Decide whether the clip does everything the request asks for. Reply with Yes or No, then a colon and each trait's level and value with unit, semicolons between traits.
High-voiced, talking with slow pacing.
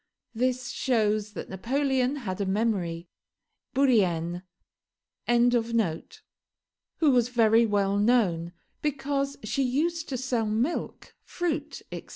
Yes: high, 235 Hz; slow, 105 wpm